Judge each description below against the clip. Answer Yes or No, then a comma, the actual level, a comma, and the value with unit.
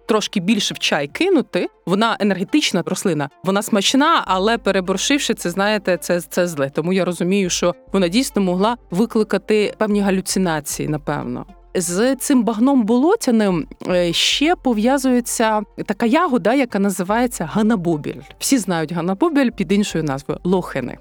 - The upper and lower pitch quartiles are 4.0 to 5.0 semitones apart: Yes, average, 4.7 semitones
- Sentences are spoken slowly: No, average, 130 wpm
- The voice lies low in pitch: No, high, 200 Hz